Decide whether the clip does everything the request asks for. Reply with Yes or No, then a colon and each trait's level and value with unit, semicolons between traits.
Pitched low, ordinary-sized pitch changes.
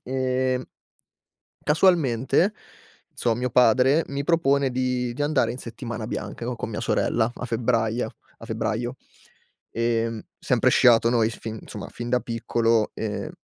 No: low, 120 Hz; narrow, 2.2 semitones